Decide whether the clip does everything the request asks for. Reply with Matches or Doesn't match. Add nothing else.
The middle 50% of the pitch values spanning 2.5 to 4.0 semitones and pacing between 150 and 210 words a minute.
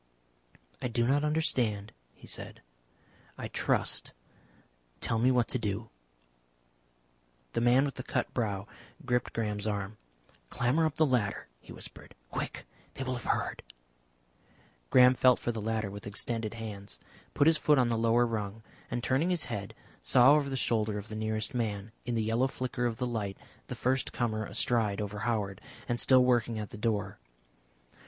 Matches